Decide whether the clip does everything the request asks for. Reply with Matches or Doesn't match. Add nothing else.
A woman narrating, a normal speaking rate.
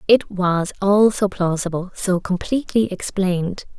Doesn't match